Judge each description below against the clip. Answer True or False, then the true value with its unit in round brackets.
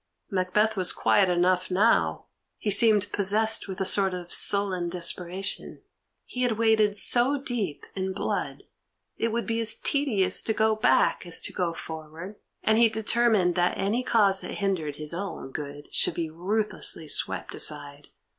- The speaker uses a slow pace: False (160 wpm)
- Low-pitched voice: False (195 Hz)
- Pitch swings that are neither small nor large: True (3.8 semitones)